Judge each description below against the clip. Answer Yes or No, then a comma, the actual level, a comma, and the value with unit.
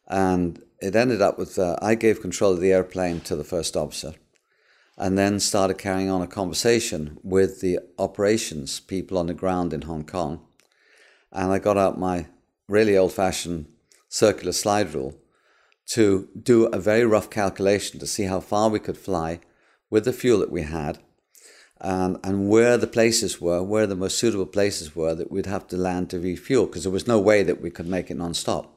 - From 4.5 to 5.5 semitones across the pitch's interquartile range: No, average, 2.8 semitones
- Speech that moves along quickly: No, average, 195 wpm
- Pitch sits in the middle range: No, very low, 95 Hz